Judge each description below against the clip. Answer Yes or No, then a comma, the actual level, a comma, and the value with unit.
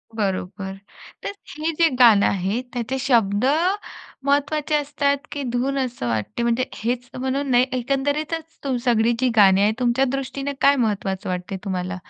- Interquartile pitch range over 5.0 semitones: Yes, wide, 5.4 semitones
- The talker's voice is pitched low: No, high, 245 Hz